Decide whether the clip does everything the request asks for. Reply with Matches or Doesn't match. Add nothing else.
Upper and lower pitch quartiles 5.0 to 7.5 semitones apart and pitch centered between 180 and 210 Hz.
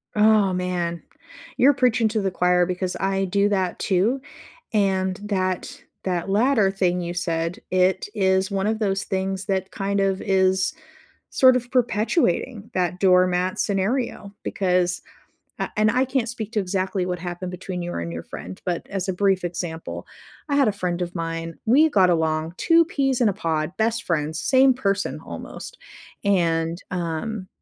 Doesn't match